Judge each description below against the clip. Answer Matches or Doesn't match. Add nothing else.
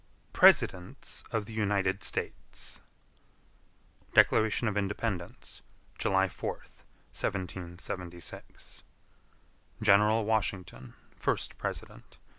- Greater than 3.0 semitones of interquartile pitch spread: Doesn't match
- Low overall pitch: Matches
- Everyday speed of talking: Doesn't match